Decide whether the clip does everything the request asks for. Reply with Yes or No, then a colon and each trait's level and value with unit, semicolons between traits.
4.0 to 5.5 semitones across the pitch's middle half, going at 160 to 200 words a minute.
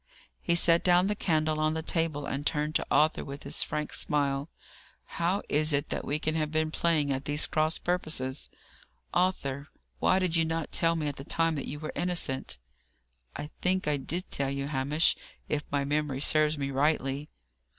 No: narrow, 2.6 semitones; average, 190 wpm